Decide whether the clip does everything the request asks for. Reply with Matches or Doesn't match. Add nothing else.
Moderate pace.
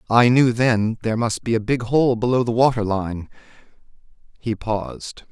Matches